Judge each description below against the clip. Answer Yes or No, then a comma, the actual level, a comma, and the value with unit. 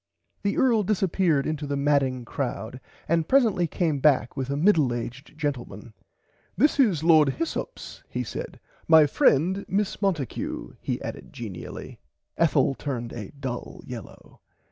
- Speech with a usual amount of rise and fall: No, wide, 6.0 semitones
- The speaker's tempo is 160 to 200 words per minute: No, average, 140 wpm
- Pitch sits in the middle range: Yes, medium, 150 Hz